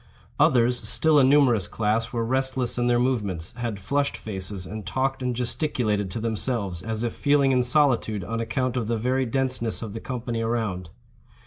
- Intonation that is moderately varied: Yes, average, 3.3 semitones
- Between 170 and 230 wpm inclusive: Yes, average, 180 wpm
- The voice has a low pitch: Yes, low, 120 Hz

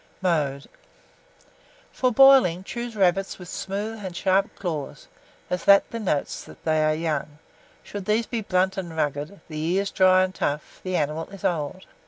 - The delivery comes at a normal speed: Yes, average, 155 wpm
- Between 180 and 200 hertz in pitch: Yes, medium, 185 Hz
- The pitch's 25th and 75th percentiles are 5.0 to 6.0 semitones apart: No, average, 4.1 semitones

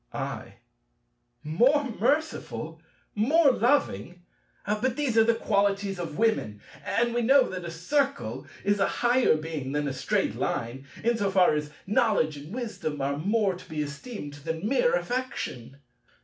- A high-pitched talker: Yes, high, 205 Hz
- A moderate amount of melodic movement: No, wide, 7.7 semitones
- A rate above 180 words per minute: No, average, 150 wpm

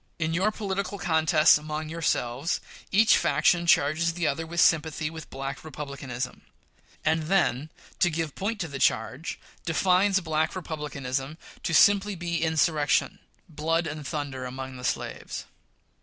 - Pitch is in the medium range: Yes, medium, 160 Hz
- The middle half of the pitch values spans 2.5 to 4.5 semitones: Yes, average, 2.9 semitones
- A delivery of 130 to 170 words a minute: Yes, average, 140 wpm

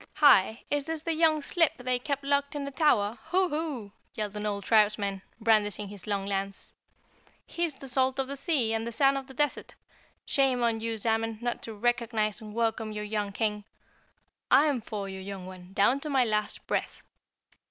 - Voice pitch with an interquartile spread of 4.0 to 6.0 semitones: Yes, average, 4.9 semitones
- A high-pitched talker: Yes, high, 230 Hz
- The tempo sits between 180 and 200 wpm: Yes, average, 190 wpm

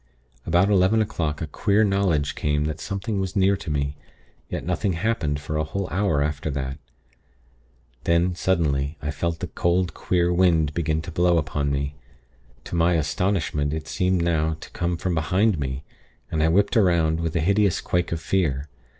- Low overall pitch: Yes, very low, 85 Hz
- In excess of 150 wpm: Yes, average, 175 wpm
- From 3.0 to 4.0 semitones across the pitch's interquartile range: Yes, average, 3.7 semitones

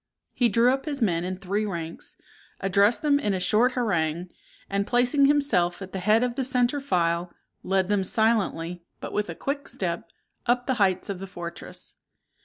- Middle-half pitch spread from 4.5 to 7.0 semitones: Yes, wide, 5.5 semitones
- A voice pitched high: Yes, high, 205 Hz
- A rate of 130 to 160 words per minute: No, average, 185 wpm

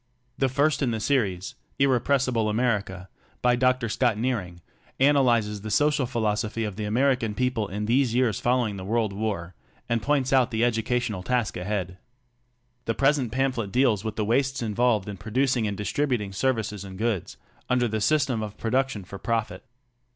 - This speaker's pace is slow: No, average, 165 wpm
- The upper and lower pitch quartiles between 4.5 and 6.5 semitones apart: No, average, 3.5 semitones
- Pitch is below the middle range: Yes, low, 115 Hz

